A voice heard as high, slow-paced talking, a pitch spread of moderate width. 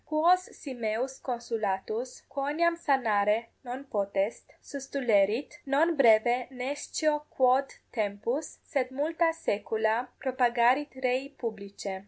Yes: very high, 255 Hz; slow, 100 wpm; average, 4.3 semitones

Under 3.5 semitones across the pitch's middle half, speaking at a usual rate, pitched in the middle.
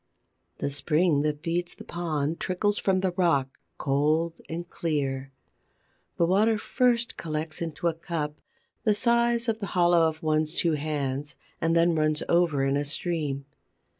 Yes: average, 2.9 semitones; average, 155 wpm; medium, 165 Hz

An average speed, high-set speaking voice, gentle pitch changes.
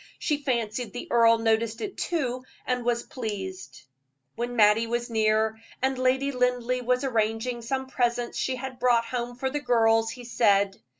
Yes: average, 165 wpm; high, 240 Hz; narrow, 2.1 semitones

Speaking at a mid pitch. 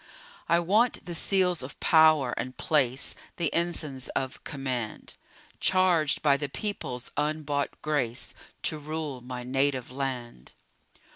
Yes: medium, 145 Hz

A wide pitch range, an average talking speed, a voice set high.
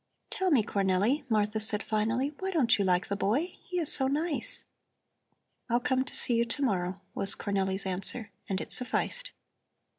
Yes: wide, 5.9 semitones; average, 175 wpm; high, 225 Hz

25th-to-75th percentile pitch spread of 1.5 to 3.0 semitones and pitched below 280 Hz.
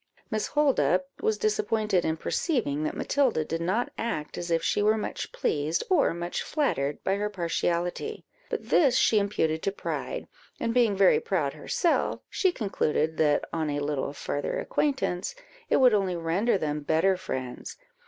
No: wide, 5.6 semitones; medium, 185 Hz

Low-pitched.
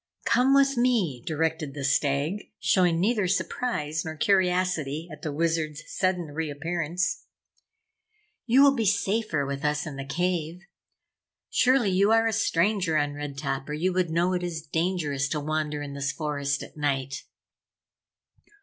No: medium, 160 Hz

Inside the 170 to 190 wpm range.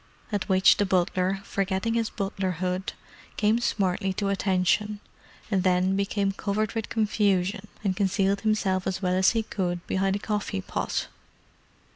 No: average, 140 wpm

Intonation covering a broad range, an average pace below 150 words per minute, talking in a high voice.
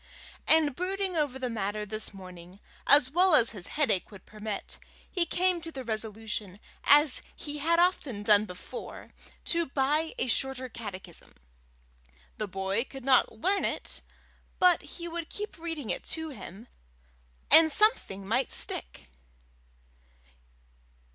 Yes: wide, 7.6 semitones; slow, 135 wpm; very high, 260 Hz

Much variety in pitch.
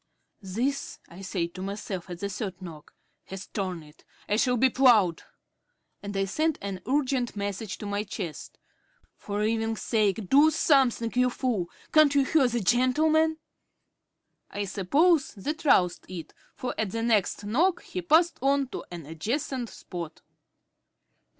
Yes: wide, 5.9 semitones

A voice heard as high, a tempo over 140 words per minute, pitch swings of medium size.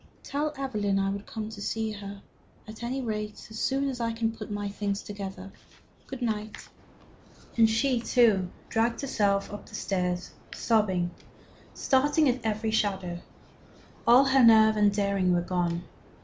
Yes: high, 215 Hz; average, 150 wpm; average, 3.0 semitones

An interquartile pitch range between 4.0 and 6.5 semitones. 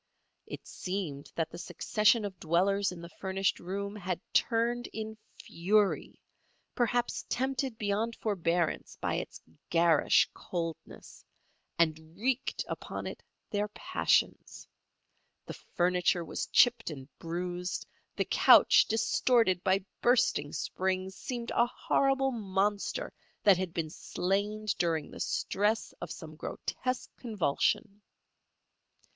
Yes: average, 4.4 semitones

